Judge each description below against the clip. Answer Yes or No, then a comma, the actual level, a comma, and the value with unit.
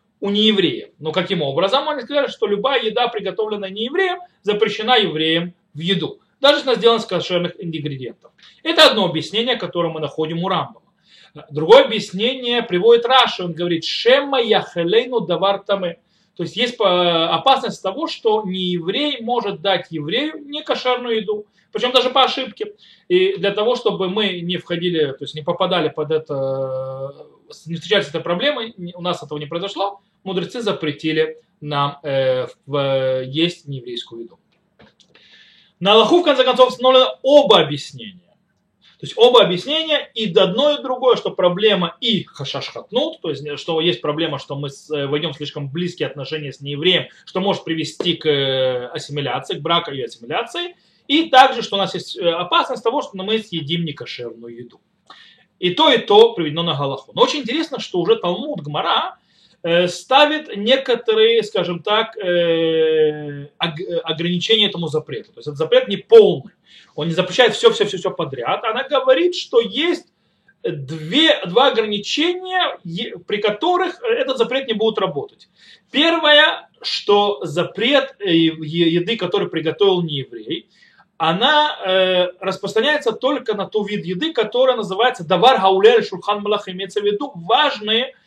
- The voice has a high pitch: Yes, high, 195 Hz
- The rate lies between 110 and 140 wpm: No, average, 150 wpm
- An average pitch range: No, wide, 7.3 semitones